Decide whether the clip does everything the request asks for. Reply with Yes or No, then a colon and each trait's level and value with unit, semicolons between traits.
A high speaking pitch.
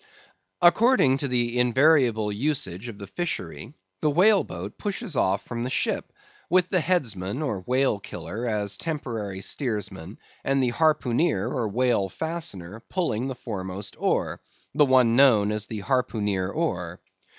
No: low, 120 Hz